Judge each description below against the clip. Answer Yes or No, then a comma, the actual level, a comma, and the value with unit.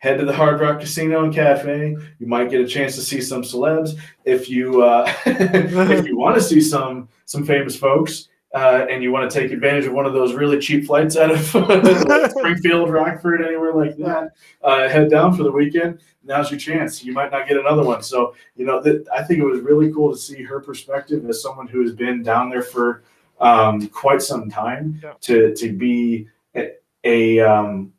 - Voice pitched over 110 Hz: Yes, medium, 140 Hz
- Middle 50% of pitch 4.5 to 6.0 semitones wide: No, average, 3.7 semitones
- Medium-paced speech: No, fast, 210 wpm